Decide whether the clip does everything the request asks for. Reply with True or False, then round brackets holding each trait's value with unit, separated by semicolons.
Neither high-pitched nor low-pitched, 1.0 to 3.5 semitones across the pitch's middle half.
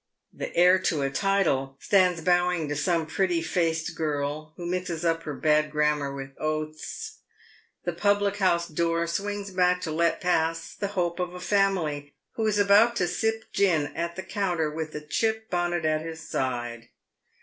True (170 Hz; 3.2 semitones)